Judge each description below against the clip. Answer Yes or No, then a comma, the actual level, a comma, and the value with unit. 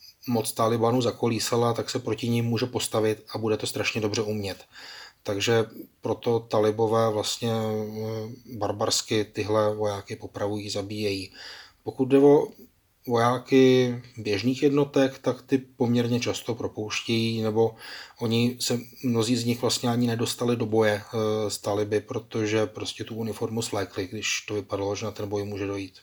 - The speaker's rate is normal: Yes, average, 145 wpm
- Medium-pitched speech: No, low, 115 Hz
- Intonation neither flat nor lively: No, narrow, 2.3 semitones